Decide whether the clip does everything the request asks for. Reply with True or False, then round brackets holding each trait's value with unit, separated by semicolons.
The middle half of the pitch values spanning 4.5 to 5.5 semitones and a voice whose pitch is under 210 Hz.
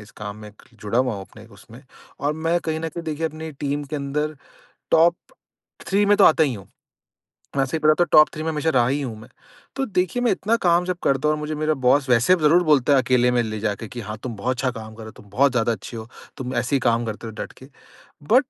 True (5.1 semitones; 140 Hz)